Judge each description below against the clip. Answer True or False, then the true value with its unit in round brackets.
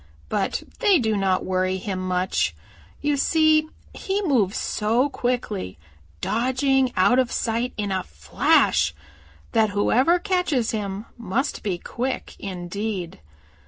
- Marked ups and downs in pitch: True (6.0 semitones)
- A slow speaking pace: True (125 wpm)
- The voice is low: False (220 Hz)